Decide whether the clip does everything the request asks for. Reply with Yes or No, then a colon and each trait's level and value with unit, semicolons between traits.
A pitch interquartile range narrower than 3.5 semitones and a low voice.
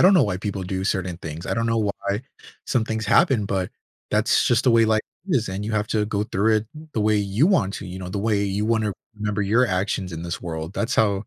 Yes: average, 2.8 semitones; low, 105 Hz